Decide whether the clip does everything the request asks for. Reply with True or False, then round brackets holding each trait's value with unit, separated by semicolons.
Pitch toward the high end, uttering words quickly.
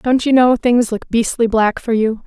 True (235 Hz; 240 wpm)